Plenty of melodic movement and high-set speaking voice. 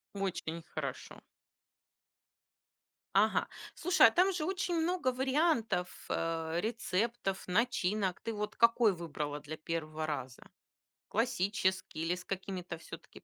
Yes: wide, 6.4 semitones; high, 195 Hz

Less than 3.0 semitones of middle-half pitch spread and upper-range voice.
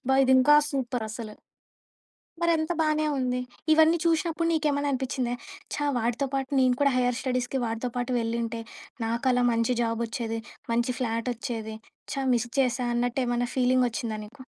Yes: narrow, 2.4 semitones; very high, 250 Hz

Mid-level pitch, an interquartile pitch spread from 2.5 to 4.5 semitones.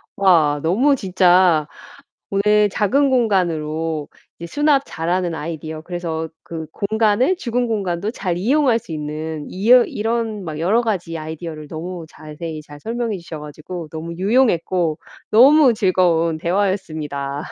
No: medium, 180 Hz; average, 5.2 semitones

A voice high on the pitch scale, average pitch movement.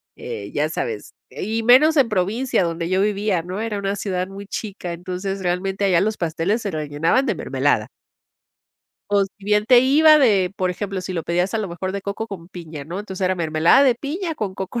Yes: high, 195 Hz; average, 3.4 semitones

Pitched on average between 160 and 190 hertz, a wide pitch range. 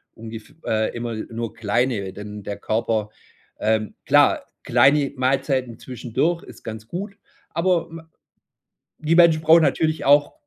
No: low, 125 Hz; wide, 6.2 semitones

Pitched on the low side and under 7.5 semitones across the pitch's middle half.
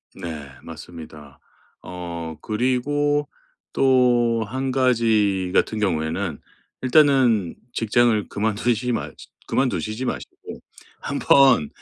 Yes: low, 110 Hz; wide, 6.4 semitones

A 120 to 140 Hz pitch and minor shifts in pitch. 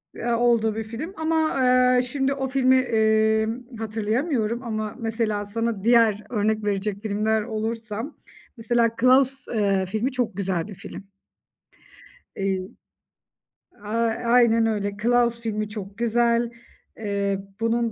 No: high, 225 Hz; narrow, 2.3 semitones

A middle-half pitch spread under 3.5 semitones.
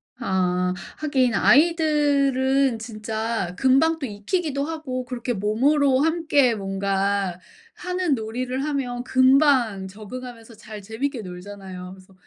No: wide, 5.4 semitones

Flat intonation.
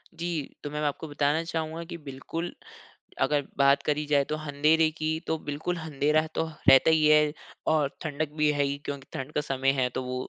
Yes: narrow, 2.0 semitones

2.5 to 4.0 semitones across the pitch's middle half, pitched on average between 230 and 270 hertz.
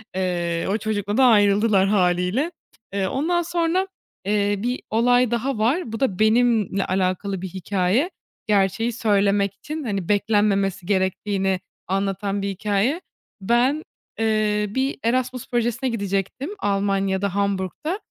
No: average, 3.6 semitones; high, 205 Hz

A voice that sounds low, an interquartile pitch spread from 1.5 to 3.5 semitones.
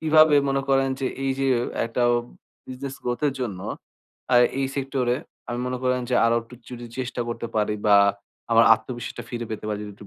Yes: low, 125 Hz; narrow, 2.6 semitones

